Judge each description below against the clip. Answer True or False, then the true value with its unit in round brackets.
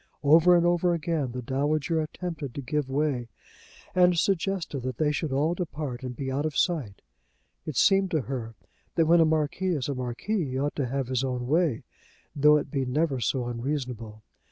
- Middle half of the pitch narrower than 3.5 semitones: False (4.3 semitones)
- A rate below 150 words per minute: False (190 wpm)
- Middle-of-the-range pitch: True (145 Hz)